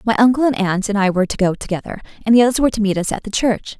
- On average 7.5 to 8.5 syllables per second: Yes, 7.7 syllables/s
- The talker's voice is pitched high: Yes, high, 215 Hz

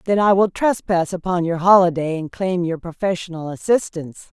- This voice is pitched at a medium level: Yes, medium, 180 Hz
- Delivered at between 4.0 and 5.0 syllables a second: No, 5.3 syllables/s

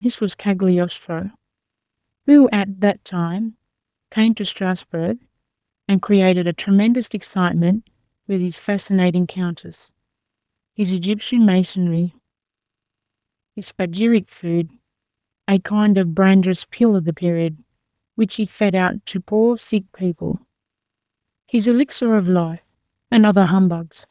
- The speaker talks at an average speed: No, slow, 120 wpm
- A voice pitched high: Yes, high, 195 Hz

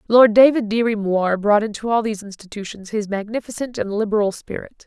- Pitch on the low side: No, high, 215 Hz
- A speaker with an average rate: Yes, average, 175 wpm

